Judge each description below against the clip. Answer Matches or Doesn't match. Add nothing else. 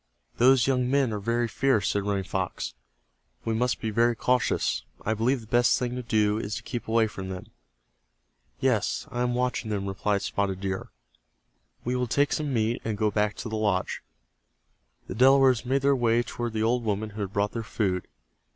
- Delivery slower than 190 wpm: Doesn't match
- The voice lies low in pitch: Matches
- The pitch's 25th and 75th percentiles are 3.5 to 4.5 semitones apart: Doesn't match